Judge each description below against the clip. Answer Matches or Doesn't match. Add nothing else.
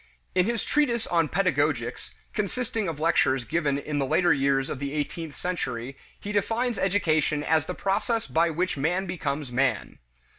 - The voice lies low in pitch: Doesn't match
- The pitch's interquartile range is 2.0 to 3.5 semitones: Doesn't match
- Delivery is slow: Doesn't match